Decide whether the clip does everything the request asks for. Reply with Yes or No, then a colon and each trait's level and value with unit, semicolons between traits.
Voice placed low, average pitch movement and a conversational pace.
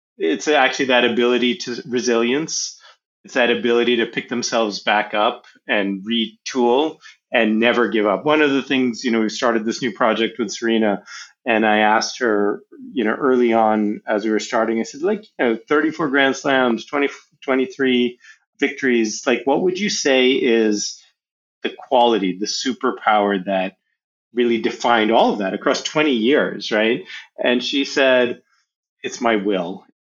Yes: low, 120 Hz; average, 3.1 semitones; average, 165 wpm